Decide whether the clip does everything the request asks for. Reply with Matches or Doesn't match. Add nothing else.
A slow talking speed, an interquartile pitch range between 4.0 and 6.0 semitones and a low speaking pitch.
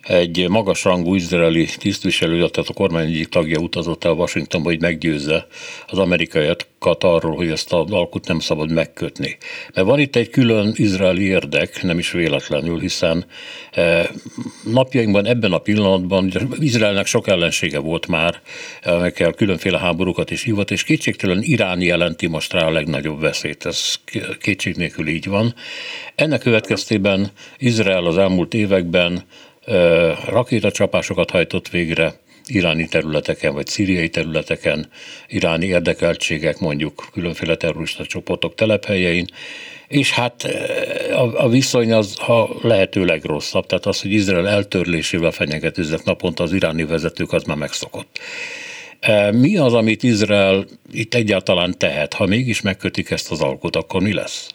Doesn't match